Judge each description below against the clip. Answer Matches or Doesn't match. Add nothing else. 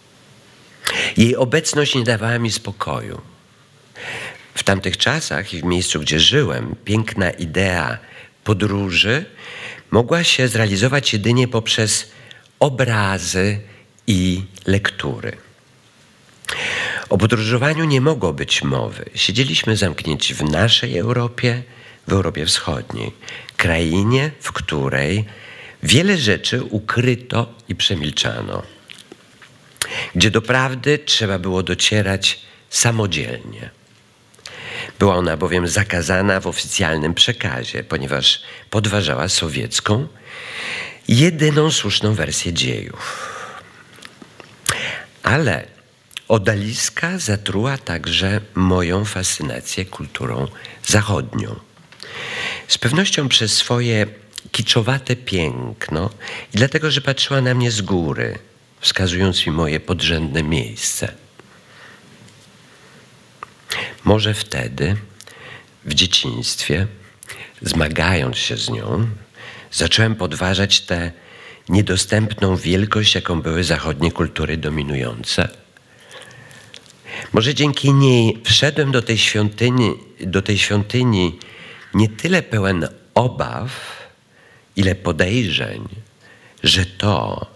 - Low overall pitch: Matches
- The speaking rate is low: Matches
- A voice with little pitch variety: Doesn't match